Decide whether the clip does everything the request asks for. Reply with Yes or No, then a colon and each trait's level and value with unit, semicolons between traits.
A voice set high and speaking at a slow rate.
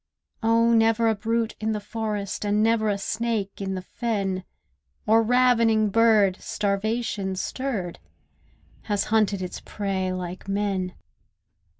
Yes: high, 210 Hz; slow, 125 wpm